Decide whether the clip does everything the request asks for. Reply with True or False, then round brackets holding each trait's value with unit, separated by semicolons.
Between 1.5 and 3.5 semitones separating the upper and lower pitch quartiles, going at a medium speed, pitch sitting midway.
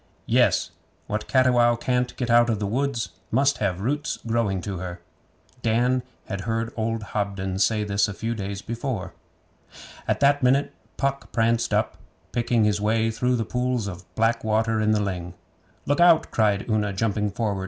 False (3.1 semitones; 170 wpm; 115 Hz)